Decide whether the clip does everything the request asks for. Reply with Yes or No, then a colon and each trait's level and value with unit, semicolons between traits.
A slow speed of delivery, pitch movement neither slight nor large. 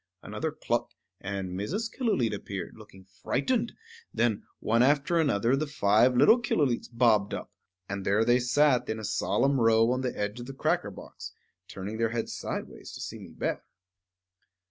No: average, 165 wpm; average, 5.0 semitones